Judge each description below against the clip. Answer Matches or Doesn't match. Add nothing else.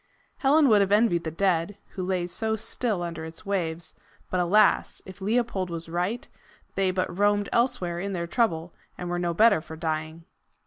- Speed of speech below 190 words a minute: Matches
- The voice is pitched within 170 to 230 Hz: Matches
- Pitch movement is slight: Doesn't match